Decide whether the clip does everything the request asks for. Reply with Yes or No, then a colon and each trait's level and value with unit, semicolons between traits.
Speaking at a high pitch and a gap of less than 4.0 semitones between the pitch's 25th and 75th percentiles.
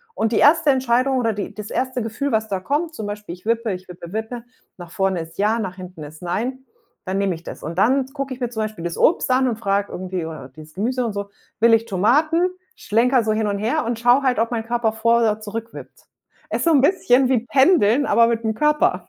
No: high, 225 Hz; average, 4.3 semitones